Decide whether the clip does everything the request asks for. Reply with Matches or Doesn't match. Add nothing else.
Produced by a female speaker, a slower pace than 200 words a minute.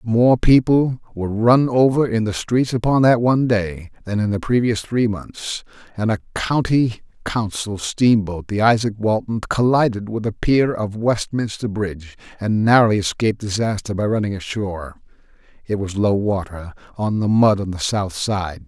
Doesn't match